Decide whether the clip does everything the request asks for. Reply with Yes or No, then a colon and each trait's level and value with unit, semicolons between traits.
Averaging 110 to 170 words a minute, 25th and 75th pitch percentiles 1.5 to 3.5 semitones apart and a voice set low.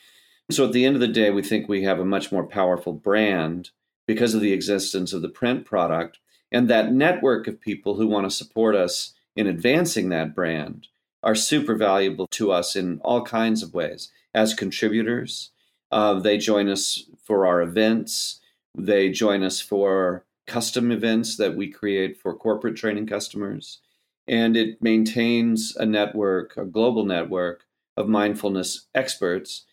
Yes: average, 165 wpm; average, 3.0 semitones; low, 105 Hz